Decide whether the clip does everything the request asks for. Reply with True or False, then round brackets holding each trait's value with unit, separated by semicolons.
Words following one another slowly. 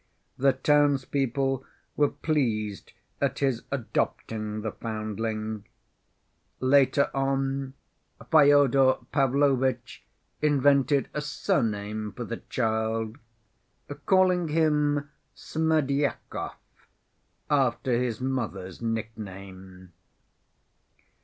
True (75 wpm)